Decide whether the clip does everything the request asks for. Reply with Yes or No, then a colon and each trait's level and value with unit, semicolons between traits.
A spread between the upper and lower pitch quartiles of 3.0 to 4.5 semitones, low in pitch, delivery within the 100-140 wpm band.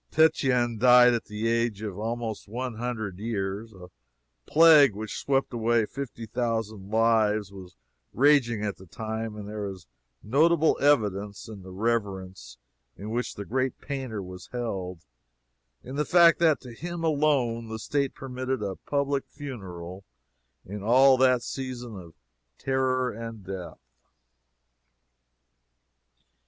Yes: average, 4.2 semitones; low, 115 Hz; slow, 135 wpm